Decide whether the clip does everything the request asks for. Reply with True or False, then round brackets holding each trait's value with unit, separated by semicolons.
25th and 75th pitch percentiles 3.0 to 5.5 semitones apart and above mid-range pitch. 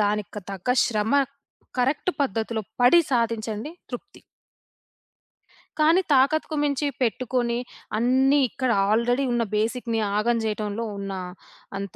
True (3.5 semitones; 235 Hz)